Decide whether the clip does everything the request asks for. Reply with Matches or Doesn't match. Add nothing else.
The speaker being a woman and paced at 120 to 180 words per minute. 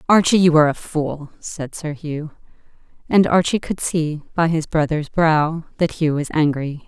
Matches